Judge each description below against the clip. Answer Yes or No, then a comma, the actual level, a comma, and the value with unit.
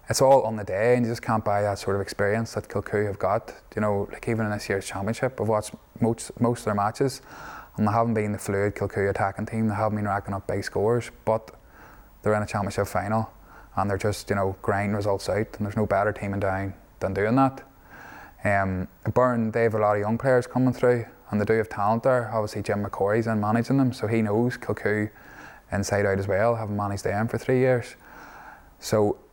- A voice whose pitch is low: Yes, low, 105 Hz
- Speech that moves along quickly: Yes, fast, 230 wpm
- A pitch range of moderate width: No, narrow, 2.3 semitones